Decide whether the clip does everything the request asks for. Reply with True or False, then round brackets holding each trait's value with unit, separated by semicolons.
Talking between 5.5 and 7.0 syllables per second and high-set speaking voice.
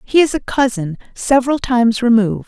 True (5.8 syllables/s; 240 Hz)